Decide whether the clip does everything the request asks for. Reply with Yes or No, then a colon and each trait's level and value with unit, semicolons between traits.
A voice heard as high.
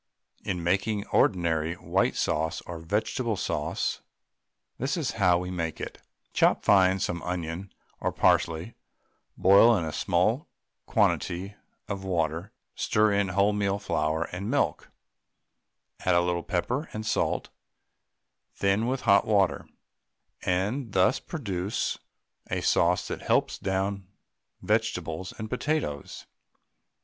No: very low, 95 Hz